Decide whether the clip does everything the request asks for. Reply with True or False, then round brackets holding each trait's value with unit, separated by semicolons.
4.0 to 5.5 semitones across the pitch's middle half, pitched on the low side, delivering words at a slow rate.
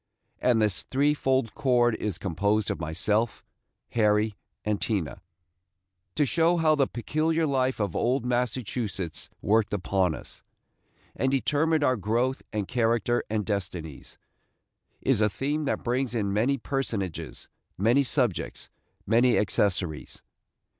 True (4.5 semitones; 115 Hz; 125 wpm)